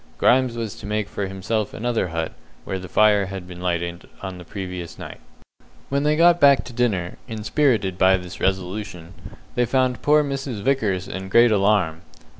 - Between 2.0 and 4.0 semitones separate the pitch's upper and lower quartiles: No, average, 4.8 semitones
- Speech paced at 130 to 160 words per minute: No, average, 175 wpm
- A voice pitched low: Yes, low, 105 Hz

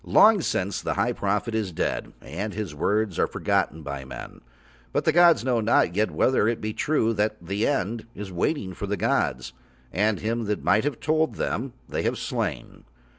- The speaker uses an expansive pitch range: No, average, 3.3 semitones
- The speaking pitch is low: Yes, low, 110 Hz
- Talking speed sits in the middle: Yes, average, 190 wpm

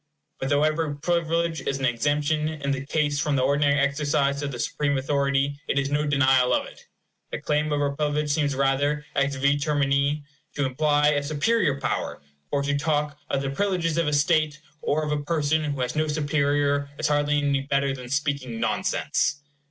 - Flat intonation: Yes, narrow, 1.3 semitones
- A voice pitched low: No, medium, 145 Hz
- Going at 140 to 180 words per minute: No, average, 190 wpm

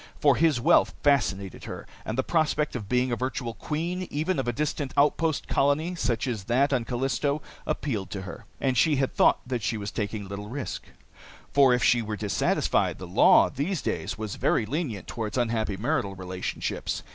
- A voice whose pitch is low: Yes, low, 125 Hz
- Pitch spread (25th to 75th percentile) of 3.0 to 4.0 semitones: No, average, 5.0 semitones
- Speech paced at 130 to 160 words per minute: No, average, 185 wpm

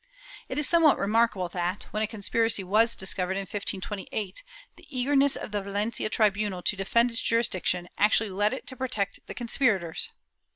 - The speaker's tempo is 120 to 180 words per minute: Yes, average, 170 wpm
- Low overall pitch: No, high, 210 Hz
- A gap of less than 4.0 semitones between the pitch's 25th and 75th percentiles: Yes, average, 3.2 semitones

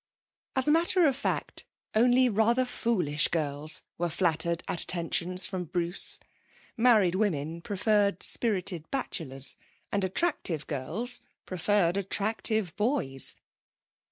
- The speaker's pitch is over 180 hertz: Yes, high, 190 Hz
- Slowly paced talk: Yes, slow, 110 wpm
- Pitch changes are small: No, wide, 5.4 semitones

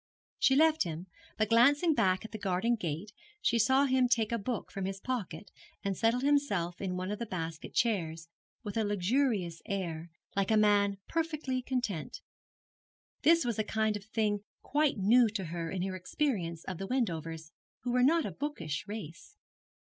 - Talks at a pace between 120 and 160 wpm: No, average, 175 wpm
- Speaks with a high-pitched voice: Yes, high, 210 Hz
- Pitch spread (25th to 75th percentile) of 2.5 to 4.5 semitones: No, wide, 5.4 semitones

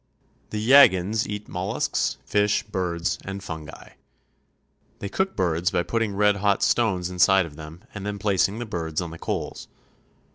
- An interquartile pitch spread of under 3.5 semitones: Yes, average, 3.0 semitones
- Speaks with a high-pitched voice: No, very low, 95 Hz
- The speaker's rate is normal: Yes, average, 155 wpm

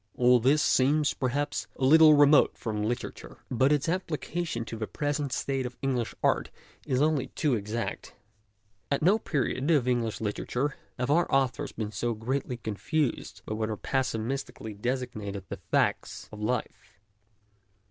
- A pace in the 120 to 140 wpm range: No, average, 160 wpm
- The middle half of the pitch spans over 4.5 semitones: No, average, 4.2 semitones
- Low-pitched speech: Yes, low, 130 Hz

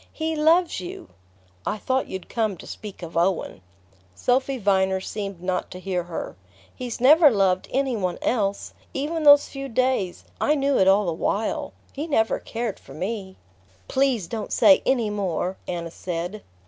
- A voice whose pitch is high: Yes, high, 210 Hz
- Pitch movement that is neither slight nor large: No, wide, 6.2 semitones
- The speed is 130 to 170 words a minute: Yes, average, 160 wpm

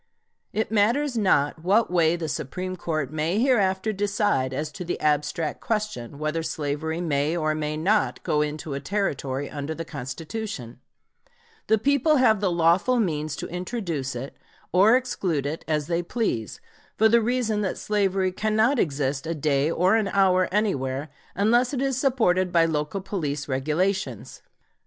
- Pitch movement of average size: No, wide, 5.9 semitones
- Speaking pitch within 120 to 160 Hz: No, medium, 175 Hz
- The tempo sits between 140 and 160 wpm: Yes, average, 155 wpm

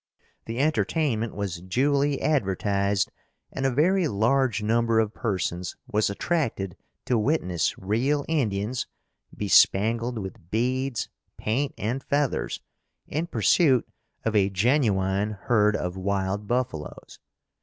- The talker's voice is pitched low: Yes, low, 110 Hz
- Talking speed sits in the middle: No, slow, 110 wpm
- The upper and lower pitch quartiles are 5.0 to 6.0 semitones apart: Yes, average, 5.3 semitones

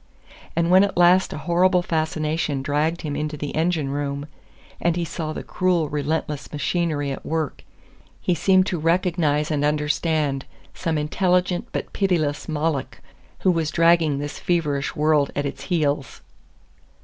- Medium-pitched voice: Yes, medium, 155 Hz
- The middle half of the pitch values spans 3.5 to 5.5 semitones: No, average, 2.9 semitones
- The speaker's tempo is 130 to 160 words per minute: Yes, average, 150 wpm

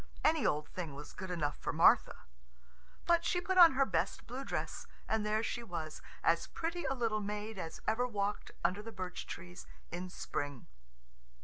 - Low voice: No, high, 210 Hz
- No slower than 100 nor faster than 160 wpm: No, average, 180 wpm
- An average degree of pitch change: No, wide, 6.0 semitones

